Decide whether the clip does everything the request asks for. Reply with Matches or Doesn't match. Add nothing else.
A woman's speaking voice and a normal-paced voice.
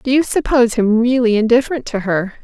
Matches